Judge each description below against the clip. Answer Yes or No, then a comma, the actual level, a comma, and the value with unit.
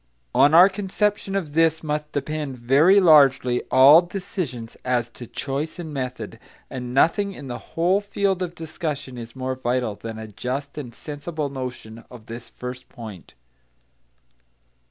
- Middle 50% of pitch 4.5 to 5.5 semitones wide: Yes, average, 4.9 semitones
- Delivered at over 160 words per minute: No, average, 150 wpm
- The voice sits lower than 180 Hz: Yes, medium, 140 Hz